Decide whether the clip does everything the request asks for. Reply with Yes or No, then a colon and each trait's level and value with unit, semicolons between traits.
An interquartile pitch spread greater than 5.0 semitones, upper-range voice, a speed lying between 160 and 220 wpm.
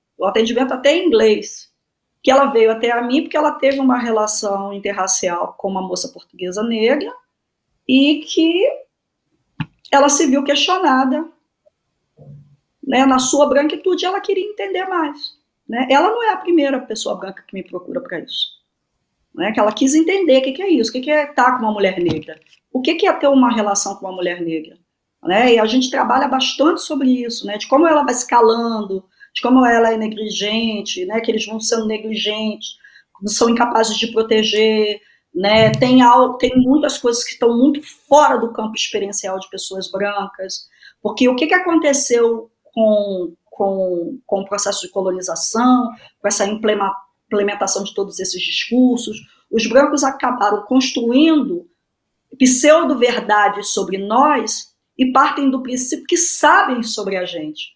Yes: wide, 5.5 semitones; high, 235 Hz; average, 165 wpm